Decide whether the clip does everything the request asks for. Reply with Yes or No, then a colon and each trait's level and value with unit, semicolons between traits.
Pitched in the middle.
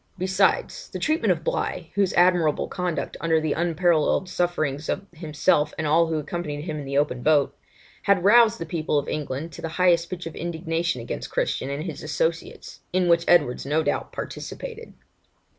Yes: medium, 165 Hz